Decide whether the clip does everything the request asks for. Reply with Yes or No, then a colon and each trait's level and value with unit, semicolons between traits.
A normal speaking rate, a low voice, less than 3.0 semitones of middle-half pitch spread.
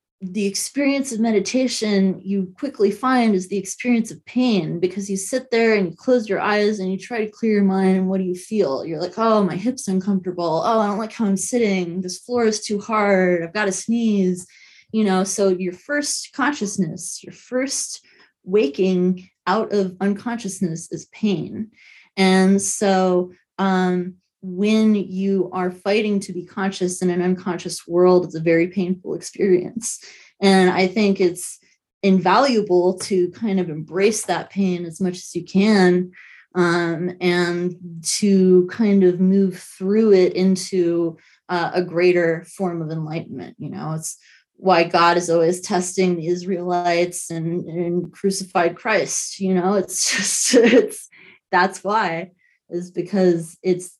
No: average, 160 wpm; medium, 185 Hz; narrow, 2.4 semitones